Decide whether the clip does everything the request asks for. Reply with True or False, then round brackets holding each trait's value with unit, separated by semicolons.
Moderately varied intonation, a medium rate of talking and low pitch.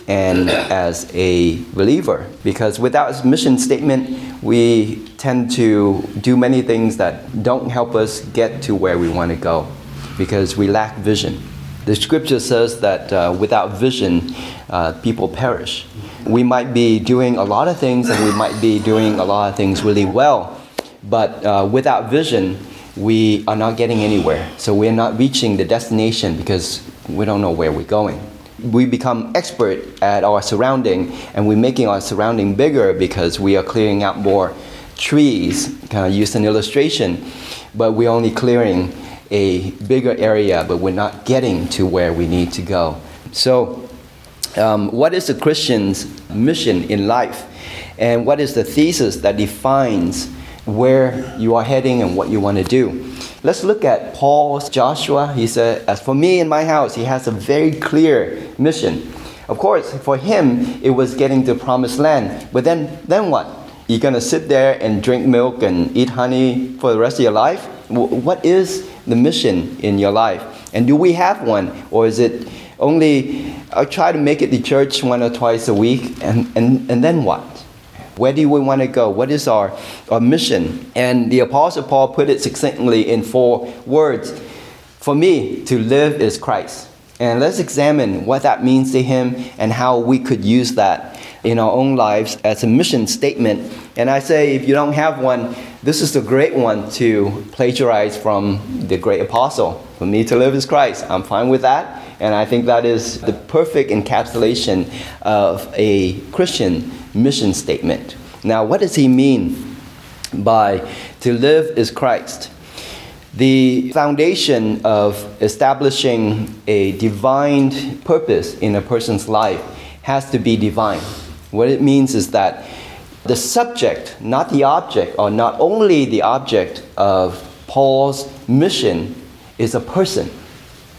True (4.1 semitones; 170 wpm; 120 Hz)